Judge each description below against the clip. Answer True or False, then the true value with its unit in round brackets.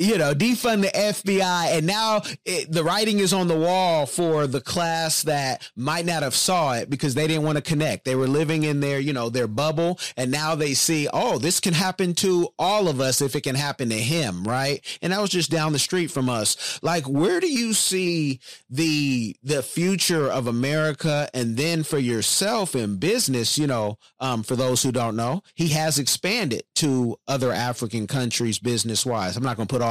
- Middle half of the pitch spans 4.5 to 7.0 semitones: True (5.1 semitones)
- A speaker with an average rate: False (210 wpm)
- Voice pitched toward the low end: False (150 Hz)